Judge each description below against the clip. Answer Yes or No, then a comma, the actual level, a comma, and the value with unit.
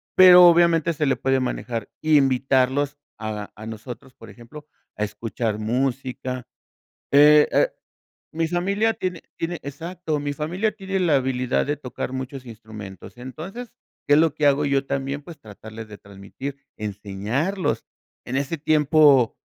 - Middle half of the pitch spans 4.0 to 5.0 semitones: Yes, average, 4.7 semitones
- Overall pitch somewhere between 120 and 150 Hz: Yes, medium, 140 Hz